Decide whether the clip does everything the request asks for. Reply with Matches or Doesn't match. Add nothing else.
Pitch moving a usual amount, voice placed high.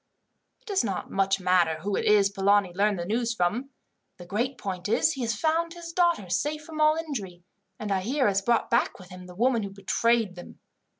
Doesn't match